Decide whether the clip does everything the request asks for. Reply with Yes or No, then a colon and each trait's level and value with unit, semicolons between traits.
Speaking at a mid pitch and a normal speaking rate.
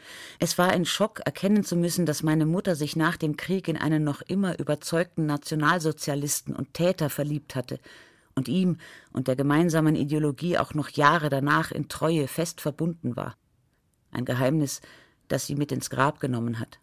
Yes: medium, 155 Hz; average, 170 wpm